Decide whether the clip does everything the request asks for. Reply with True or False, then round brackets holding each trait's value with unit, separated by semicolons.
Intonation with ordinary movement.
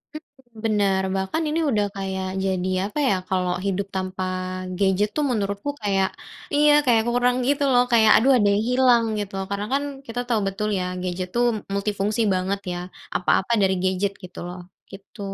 True (4.0 semitones)